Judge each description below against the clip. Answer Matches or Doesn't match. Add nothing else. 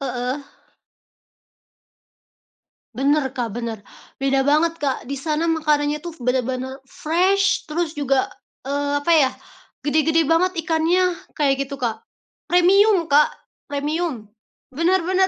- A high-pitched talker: Matches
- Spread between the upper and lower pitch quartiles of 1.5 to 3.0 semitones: Doesn't match